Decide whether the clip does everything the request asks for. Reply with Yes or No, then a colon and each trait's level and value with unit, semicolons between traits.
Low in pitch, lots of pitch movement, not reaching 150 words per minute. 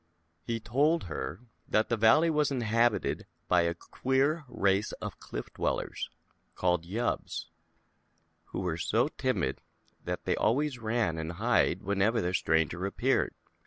Yes: low, 110 Hz; wide, 6.2 semitones; average, 140 wpm